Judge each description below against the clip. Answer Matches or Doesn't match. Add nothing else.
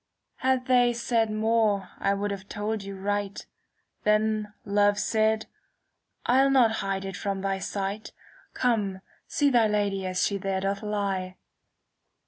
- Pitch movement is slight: Matches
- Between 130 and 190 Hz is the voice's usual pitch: Doesn't match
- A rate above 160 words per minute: Doesn't match